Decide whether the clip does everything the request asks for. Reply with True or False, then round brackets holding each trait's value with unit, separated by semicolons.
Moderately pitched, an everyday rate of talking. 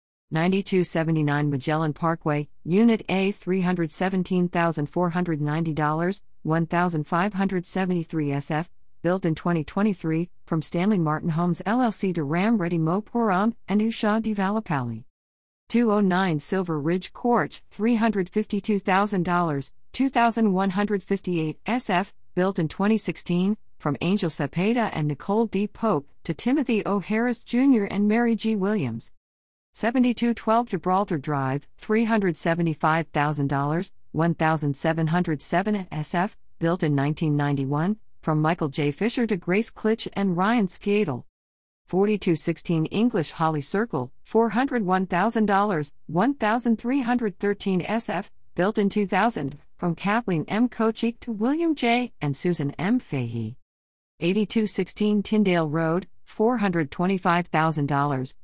False (180 Hz; 95 wpm)